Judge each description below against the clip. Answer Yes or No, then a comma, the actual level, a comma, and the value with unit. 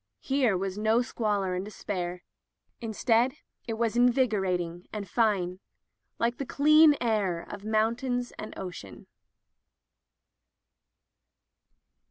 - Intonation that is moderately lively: Yes, average, 4.2 semitones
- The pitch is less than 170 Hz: No, high, 215 Hz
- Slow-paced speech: Yes, slow, 110 wpm